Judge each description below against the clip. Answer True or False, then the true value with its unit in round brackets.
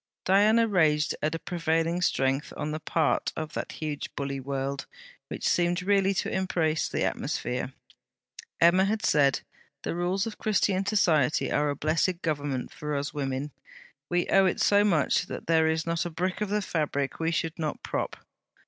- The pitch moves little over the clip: False (3.9 semitones)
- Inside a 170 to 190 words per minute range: True (175 wpm)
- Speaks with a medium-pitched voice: True (165 Hz)